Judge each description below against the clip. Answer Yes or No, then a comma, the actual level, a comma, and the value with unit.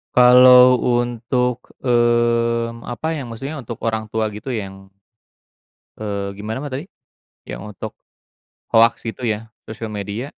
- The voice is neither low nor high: No, low, 115 Hz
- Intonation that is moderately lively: No, narrow, 2.2 semitones